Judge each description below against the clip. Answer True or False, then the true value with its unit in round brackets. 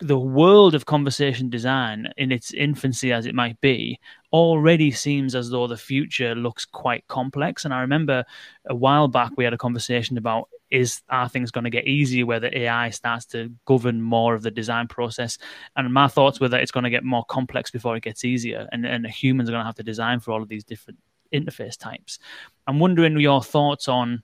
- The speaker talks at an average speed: False (215 wpm)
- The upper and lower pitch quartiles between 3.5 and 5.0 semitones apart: False (2.6 semitones)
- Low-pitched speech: True (125 Hz)